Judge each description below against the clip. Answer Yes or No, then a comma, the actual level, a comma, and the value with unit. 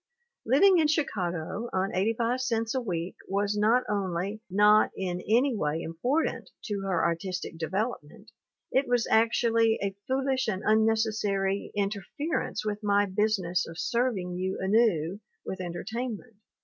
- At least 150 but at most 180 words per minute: No, average, 140 wpm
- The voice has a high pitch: Yes, high, 210 Hz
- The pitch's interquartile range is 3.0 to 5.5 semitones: Yes, average, 3.6 semitones